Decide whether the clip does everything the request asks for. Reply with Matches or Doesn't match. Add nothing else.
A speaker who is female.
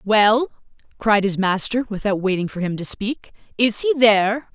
Matches